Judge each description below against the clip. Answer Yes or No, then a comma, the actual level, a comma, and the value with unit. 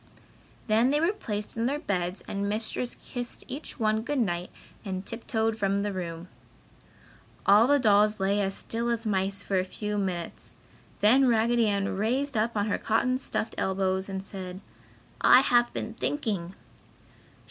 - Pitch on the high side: Yes, high, 210 Hz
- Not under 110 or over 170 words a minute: Yes, average, 160 wpm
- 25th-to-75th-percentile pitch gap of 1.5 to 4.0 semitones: Yes, average, 3.5 semitones